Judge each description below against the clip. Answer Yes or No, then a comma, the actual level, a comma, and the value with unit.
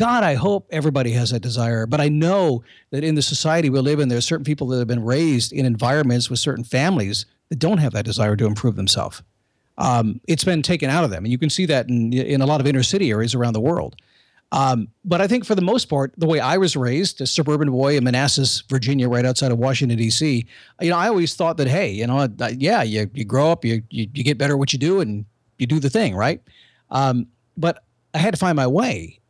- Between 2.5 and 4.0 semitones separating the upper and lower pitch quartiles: No, average, 4.6 semitones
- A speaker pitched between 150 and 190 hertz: No, low, 135 Hz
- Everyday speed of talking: No, fast, 250 wpm